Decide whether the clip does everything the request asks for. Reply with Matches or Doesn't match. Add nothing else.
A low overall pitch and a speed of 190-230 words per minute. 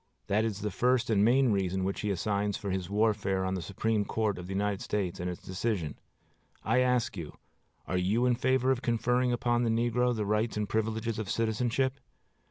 Matches